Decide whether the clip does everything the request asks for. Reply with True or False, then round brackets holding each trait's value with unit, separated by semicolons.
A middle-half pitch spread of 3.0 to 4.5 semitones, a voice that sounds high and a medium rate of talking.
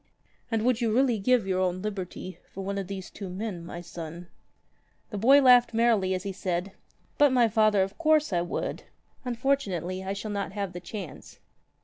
True (4.1 semitones; 200 Hz; 190 wpm)